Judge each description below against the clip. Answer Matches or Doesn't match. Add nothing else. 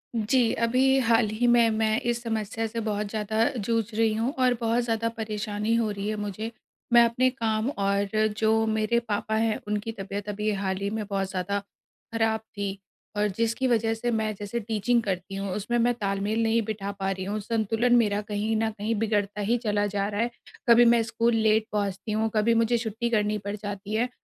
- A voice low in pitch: Doesn't match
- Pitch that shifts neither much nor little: Doesn't match